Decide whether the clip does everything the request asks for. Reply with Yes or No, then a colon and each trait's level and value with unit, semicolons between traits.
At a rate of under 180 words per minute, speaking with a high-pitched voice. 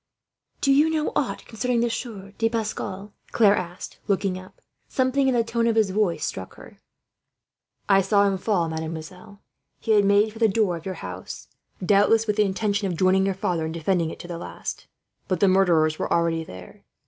No: average, 195 wpm; high, 195 Hz